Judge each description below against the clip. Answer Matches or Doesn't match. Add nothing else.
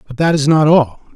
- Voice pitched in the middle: Matches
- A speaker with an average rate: Doesn't match